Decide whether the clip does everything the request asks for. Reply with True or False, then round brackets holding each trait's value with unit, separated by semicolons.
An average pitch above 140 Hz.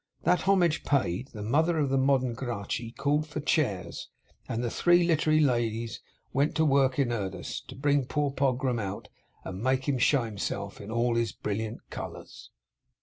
False (130 Hz)